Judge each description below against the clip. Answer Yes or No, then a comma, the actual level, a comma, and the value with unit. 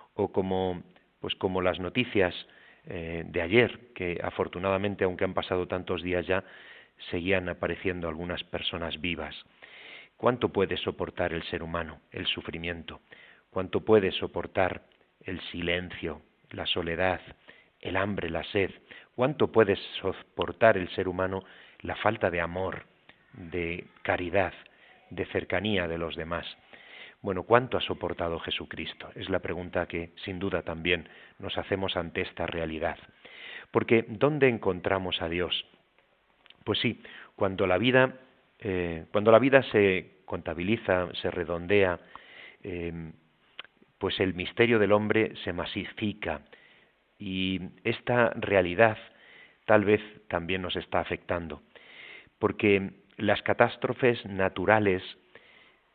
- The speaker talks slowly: Yes, slow, 120 wpm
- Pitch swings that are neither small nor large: Yes, average, 3.0 semitones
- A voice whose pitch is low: Yes, very low, 90 Hz